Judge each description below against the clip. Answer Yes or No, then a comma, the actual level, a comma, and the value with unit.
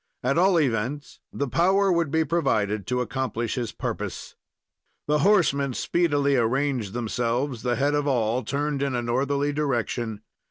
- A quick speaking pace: No, average, 150 wpm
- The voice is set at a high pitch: No, low, 135 Hz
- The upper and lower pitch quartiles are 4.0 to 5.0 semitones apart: No, average, 3.6 semitones